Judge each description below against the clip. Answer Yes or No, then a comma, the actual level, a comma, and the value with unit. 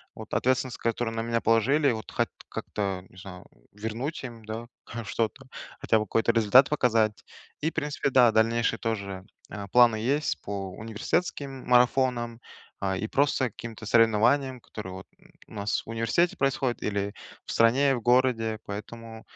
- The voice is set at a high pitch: No, low, 115 Hz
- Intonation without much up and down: No, average, 3.0 semitones